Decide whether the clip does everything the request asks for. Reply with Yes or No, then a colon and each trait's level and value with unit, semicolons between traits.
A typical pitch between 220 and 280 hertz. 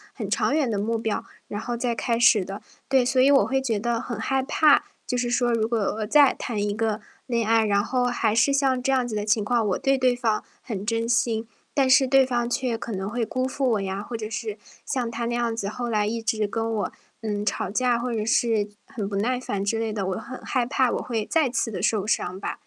Yes: high, 230 Hz